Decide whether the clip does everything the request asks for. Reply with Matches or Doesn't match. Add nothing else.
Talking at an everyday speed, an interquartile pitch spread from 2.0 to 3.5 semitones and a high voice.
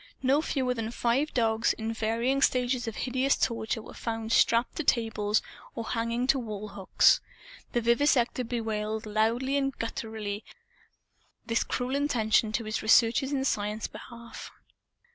Matches